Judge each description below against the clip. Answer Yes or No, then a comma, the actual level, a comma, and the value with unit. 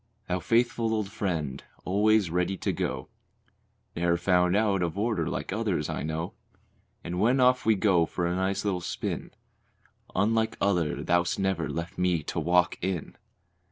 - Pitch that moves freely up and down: No, average, 3.6 semitones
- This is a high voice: No, very low, 90 Hz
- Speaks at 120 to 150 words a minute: No, average, 160 wpm